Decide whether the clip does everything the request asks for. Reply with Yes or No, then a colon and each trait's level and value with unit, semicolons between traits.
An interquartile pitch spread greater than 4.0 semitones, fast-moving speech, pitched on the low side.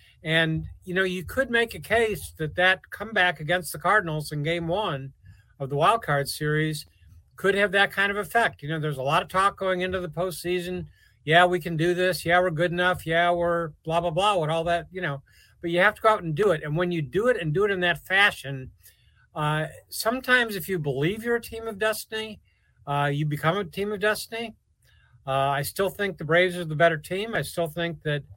No: average, 4.4 semitones; fast, 230 wpm; medium, 175 Hz